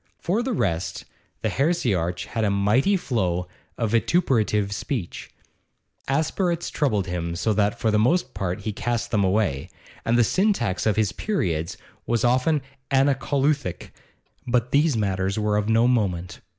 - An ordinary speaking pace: Yes, average, 150 wpm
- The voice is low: Yes, low, 110 Hz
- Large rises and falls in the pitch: Yes, wide, 6.1 semitones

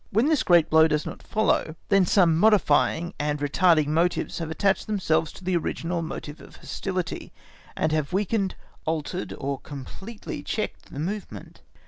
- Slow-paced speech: No, average, 155 wpm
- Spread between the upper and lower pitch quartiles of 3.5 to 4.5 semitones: Yes, average, 3.9 semitones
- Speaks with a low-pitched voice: No, medium, 170 Hz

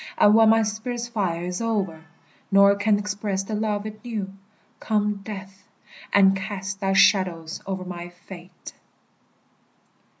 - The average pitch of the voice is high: Yes, high, 200 Hz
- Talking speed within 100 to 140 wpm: Yes, slow, 135 wpm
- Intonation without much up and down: Yes, narrow, 2.0 semitones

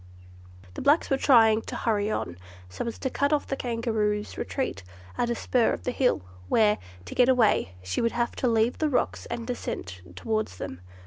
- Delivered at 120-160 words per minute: No, average, 195 wpm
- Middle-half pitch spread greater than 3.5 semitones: No, average, 3.2 semitones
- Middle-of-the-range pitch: No, high, 230 Hz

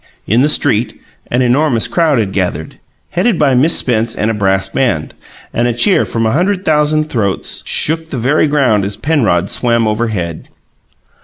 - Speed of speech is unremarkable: Yes, average, 170 wpm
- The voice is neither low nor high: No, low, 120 Hz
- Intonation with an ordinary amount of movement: No, wide, 6.0 semitones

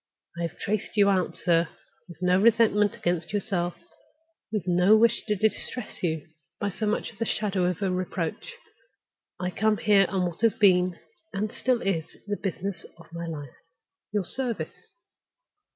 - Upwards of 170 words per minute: No, average, 160 wpm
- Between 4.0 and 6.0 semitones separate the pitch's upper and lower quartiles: No, average, 3.3 semitones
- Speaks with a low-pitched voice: No, high, 195 Hz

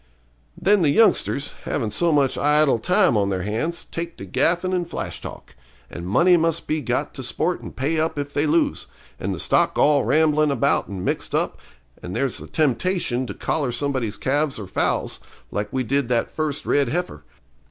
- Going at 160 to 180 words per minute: No, average, 190 wpm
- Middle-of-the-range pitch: Yes, medium, 145 Hz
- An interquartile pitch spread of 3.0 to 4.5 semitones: No, average, 5.2 semitones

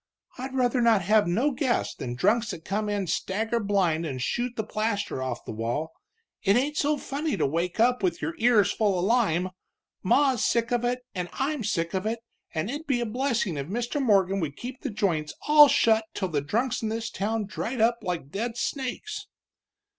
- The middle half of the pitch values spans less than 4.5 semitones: No, average, 5.3 semitones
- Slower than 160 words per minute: No, fast, 205 wpm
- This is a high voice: Yes, high, 220 Hz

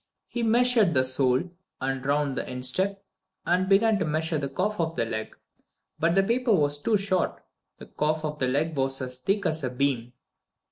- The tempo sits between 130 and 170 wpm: No, average, 190 wpm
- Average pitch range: No, wide, 6.6 semitones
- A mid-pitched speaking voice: Yes, medium, 155 Hz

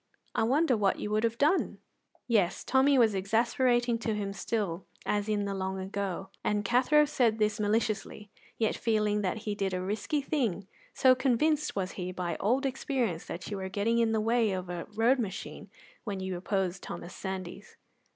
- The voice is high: Yes, high, 210 Hz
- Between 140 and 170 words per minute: No, average, 180 wpm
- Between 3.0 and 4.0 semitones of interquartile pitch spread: Yes, average, 3.7 semitones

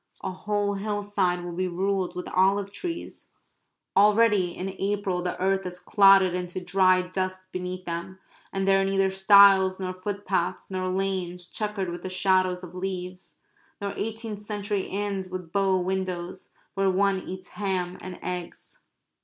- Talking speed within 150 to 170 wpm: Yes, average, 155 wpm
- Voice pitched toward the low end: No, high, 190 Hz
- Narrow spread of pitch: Yes, narrow, 1.4 semitones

